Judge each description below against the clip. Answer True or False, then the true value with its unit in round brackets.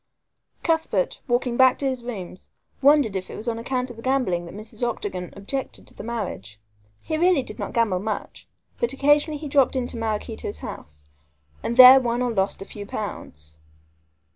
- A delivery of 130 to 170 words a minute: False (180 wpm)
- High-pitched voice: True (235 Hz)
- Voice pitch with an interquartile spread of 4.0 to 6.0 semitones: True (4.6 semitones)